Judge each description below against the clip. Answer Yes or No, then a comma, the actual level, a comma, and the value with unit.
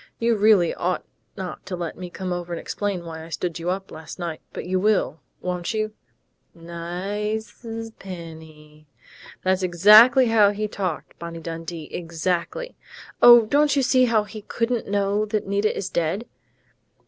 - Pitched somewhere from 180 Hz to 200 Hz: Yes, high, 190 Hz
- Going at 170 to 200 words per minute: No, average, 160 wpm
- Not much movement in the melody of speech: No, average, 4.1 semitones